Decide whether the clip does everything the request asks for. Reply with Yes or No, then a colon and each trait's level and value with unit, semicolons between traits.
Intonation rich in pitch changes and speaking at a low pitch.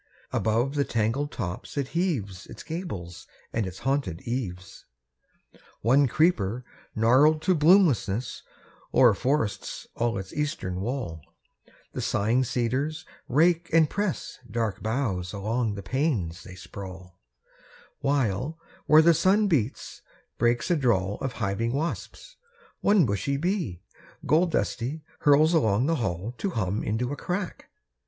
Yes: wide, 7.2 semitones; low, 125 Hz